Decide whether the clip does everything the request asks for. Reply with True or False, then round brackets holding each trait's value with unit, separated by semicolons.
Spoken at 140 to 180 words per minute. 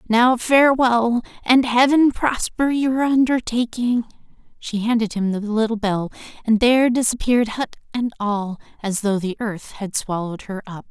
True (150 wpm)